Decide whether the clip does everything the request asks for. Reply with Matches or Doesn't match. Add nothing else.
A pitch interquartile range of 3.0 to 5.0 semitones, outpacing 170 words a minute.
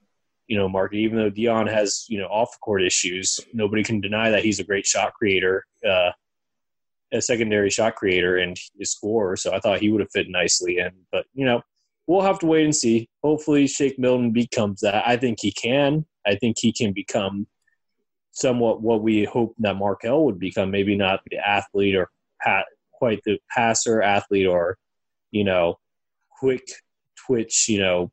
Matches